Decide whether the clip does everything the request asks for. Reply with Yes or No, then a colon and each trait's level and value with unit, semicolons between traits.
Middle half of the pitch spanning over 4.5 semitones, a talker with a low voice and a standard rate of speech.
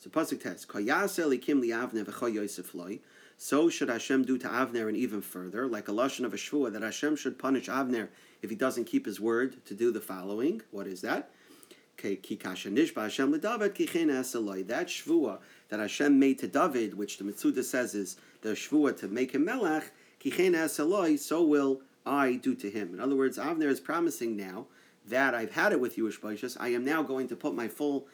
Yes: average, 4.9 semitones; low, 130 Hz; average, 175 wpm